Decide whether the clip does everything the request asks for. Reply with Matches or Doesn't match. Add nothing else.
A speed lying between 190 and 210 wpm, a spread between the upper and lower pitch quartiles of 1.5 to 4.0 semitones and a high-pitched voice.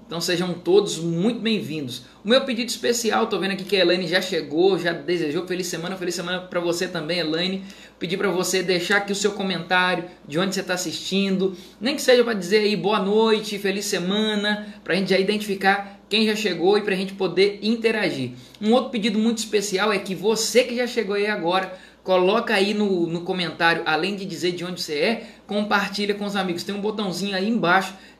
Matches